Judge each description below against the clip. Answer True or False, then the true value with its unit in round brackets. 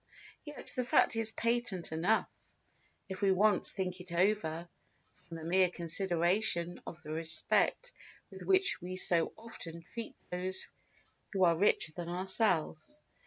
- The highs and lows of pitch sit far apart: False (4.1 semitones)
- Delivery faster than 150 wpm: False (140 wpm)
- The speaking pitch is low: False (185 Hz)